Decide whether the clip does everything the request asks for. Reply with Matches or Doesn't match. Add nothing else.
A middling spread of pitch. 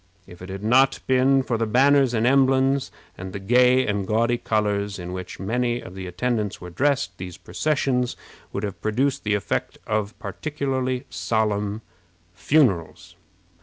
Matches